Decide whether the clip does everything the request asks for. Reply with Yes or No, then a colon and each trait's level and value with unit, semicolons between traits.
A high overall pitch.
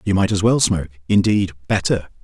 No: very low, 95 Hz